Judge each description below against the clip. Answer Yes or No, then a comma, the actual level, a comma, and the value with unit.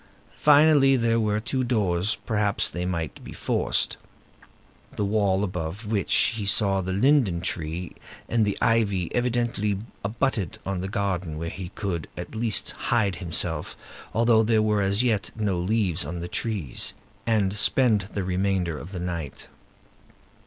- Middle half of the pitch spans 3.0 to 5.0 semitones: Yes, average, 3.8 semitones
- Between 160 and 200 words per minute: No, average, 150 wpm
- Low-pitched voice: Yes, low, 100 Hz